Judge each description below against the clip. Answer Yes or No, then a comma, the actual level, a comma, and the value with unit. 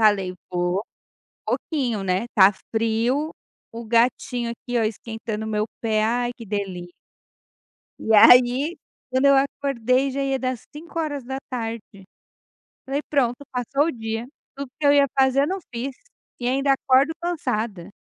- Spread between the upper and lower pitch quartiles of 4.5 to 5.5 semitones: No, average, 3.8 semitones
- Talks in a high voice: Yes, high, 245 Hz